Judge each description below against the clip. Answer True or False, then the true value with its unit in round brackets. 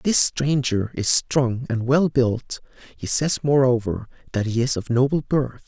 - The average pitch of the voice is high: False (130 Hz)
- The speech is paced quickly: False (170 wpm)